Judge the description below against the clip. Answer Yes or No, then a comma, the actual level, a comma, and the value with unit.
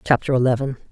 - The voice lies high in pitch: No, low, 130 Hz